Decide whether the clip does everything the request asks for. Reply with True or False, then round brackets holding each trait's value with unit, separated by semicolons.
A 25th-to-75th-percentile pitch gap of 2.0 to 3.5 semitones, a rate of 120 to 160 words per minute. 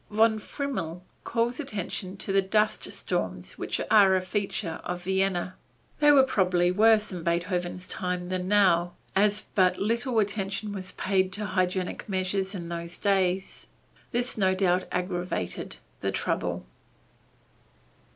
True (2.6 semitones; 135 wpm)